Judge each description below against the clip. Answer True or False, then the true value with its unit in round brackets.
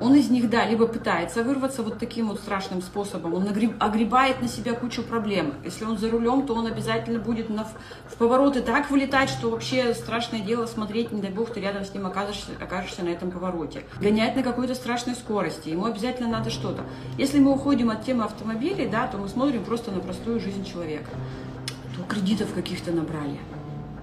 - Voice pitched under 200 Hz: False (225 Hz)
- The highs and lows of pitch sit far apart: False (3.5 semitones)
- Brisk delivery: True (185 wpm)